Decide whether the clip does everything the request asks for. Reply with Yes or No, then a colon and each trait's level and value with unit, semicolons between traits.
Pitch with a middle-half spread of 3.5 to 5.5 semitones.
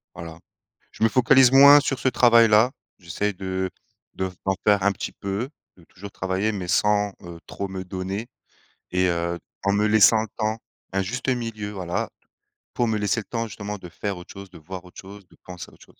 No: average, 3.1 semitones